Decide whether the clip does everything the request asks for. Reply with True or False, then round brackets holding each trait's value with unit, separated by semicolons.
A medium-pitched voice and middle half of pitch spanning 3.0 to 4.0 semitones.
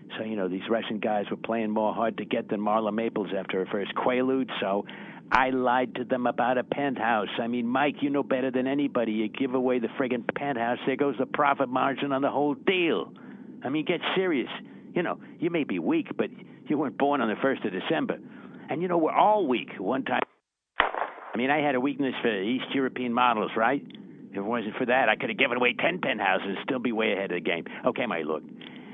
False (125 Hz; 3.7 semitones)